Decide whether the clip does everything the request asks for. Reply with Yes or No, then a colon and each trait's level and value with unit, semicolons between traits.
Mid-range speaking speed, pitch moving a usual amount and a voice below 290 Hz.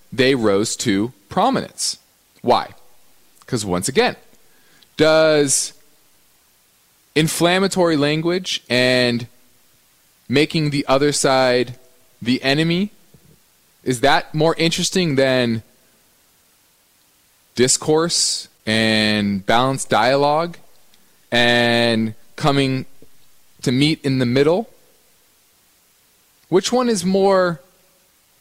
No: slow, 80 wpm; average, 4.7 semitones; medium, 140 Hz